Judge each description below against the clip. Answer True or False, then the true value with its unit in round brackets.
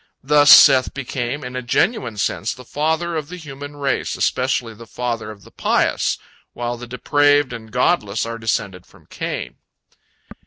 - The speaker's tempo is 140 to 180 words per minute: True (160 wpm)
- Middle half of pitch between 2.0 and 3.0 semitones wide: False (3.9 semitones)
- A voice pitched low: True (125 Hz)